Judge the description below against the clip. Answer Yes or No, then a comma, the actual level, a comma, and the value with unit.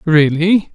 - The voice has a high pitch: No, medium, 165 Hz